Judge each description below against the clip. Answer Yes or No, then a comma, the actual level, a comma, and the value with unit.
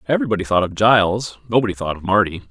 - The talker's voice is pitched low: Yes, low, 105 Hz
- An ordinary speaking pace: Yes, average, 190 wpm